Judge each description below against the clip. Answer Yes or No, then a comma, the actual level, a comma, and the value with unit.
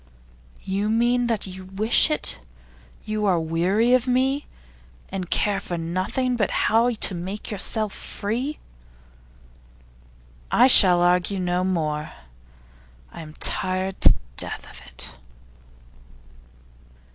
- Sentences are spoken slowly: Yes, slow, 115 wpm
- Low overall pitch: No, high, 195 Hz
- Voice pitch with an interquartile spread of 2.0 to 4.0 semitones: No, average, 4.4 semitones